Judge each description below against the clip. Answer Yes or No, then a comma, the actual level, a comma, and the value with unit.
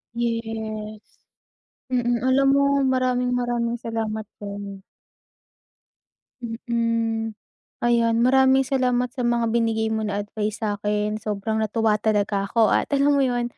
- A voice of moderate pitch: No, high, 230 Hz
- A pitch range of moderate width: No, narrow, 2.1 semitones